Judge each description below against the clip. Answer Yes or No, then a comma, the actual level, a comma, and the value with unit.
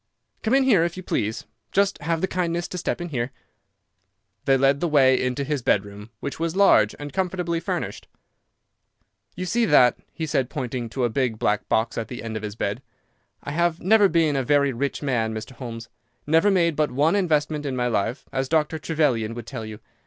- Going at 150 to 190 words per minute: No, average, 200 wpm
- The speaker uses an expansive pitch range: Yes, wide, 5.9 semitones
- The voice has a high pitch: No, medium, 140 Hz